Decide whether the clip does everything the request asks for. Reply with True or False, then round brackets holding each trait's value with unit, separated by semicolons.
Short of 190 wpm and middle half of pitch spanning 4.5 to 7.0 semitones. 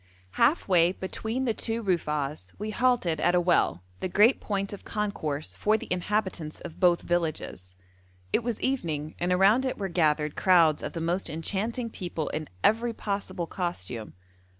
True (165 wpm; 5.1 semitones)